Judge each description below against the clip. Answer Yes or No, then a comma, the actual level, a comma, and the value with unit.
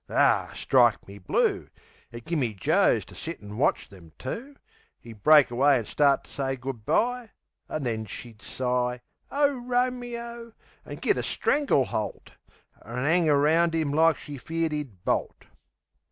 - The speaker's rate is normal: Yes, average, 165 wpm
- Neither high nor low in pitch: Yes, medium, 145 Hz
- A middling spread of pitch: No, wide, 6.3 semitones